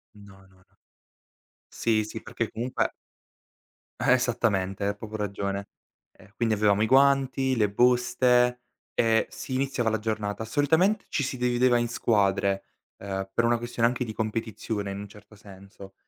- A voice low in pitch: Yes, low, 110 Hz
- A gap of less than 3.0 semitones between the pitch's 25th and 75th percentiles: No, average, 3.4 semitones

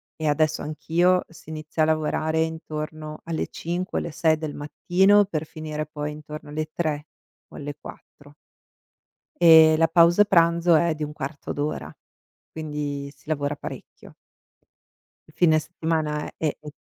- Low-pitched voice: No, medium, 155 Hz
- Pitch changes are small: Yes, narrow, 1.6 semitones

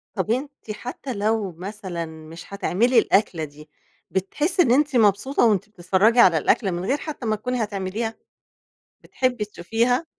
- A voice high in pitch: Yes, high, 210 Hz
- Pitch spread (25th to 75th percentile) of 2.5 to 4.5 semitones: No, average, 4.9 semitones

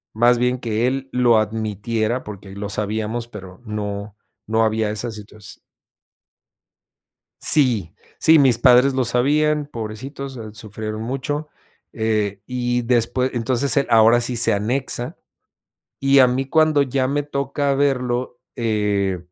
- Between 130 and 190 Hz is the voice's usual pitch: No, low, 120 Hz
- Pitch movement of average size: Yes, average, 3.7 semitones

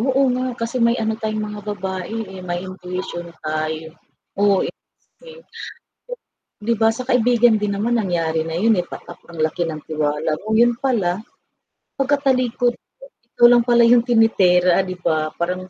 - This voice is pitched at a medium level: No, high, 210 Hz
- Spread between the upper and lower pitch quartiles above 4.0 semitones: Yes, wide, 5.5 semitones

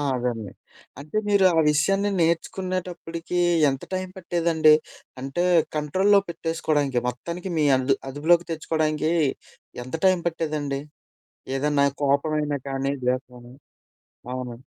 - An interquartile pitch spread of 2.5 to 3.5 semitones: No, average, 4.0 semitones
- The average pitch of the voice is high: No, medium, 155 Hz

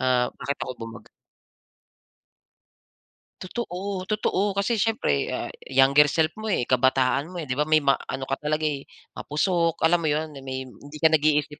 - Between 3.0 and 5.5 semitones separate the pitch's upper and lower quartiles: Yes, average, 4.2 semitones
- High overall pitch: No, medium, 150 Hz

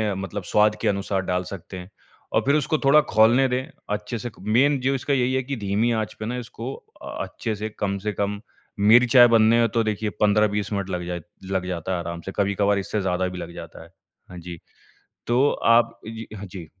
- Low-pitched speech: Yes, low, 105 Hz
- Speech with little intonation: No, average, 3.6 semitones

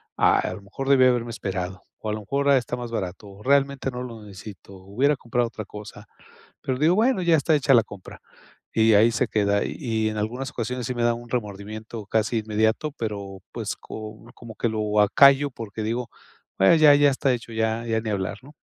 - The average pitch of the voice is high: No, low, 115 Hz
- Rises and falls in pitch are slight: No, average, 3.4 semitones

